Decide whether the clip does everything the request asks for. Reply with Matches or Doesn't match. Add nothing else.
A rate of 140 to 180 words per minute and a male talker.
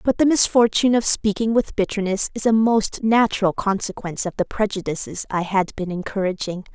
Doesn't match